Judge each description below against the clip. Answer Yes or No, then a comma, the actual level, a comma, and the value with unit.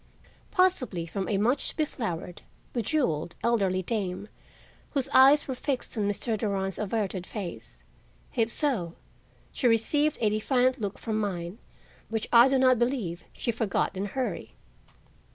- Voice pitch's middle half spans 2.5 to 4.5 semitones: No, average, 5.0 semitones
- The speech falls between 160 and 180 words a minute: No, average, 140 wpm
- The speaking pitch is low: No, high, 220 Hz